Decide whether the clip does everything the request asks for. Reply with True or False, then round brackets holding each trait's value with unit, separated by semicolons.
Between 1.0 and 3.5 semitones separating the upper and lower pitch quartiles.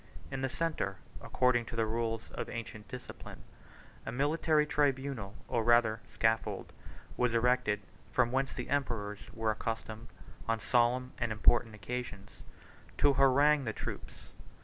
True (3.0 semitones)